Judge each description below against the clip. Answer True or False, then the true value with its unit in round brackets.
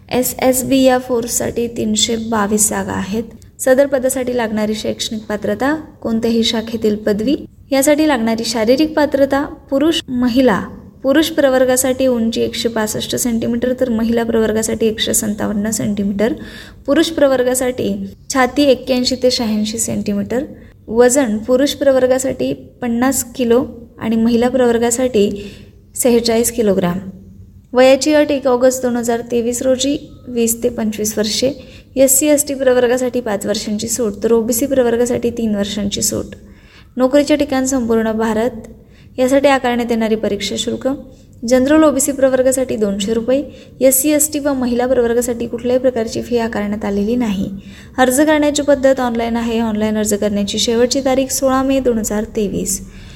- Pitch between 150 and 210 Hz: False (245 Hz)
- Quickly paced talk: True (135 wpm)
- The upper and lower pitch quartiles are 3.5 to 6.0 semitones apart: False (2.7 semitones)